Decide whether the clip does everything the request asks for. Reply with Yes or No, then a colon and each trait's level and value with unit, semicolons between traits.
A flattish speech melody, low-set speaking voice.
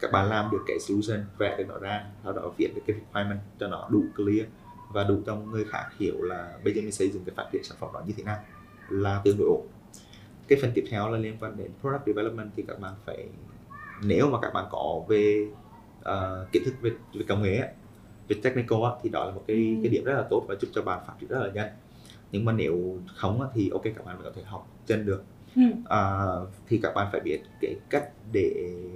Yes: narrow, 1.9 semitones; low, 105 Hz